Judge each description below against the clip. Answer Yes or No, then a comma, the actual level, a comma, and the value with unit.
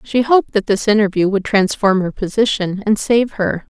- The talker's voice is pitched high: Yes, high, 210 Hz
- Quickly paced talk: No, average, 190 wpm